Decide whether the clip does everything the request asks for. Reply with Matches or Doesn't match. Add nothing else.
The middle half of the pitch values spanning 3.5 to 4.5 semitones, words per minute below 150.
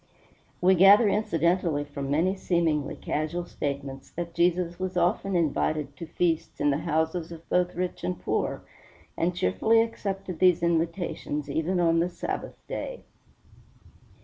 Doesn't match